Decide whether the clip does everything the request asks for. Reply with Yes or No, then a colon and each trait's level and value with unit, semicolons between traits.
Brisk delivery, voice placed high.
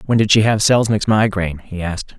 No: fast, 220 wpm; low, 105 Hz